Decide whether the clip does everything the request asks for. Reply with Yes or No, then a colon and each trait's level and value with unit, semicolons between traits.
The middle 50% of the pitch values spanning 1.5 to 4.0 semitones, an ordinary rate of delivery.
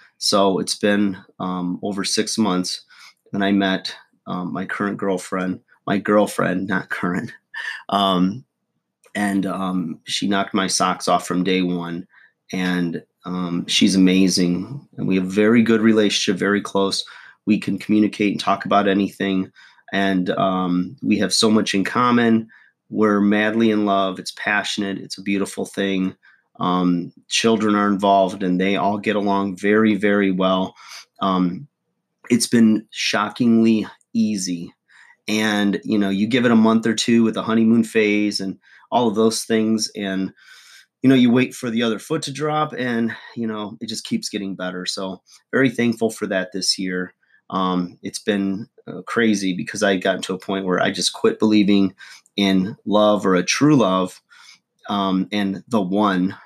Yes: narrow, 2.6 semitones; average, 165 wpm